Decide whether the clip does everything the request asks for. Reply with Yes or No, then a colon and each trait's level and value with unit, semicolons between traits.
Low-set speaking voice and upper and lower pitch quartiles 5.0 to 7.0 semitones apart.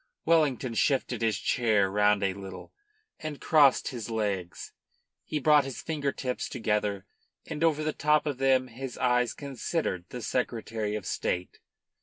Yes: low, 125 Hz; average, 5.3 semitones